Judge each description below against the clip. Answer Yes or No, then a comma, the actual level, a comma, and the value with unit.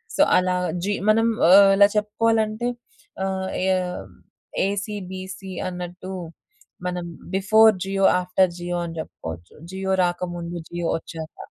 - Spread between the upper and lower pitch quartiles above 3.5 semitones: No, narrow, 2.5 semitones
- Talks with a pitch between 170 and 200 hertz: Yes, high, 190 Hz